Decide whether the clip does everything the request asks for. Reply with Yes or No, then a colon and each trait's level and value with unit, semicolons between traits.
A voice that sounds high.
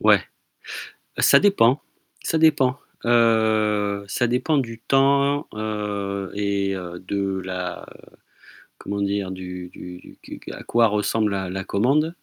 No: low, 105 Hz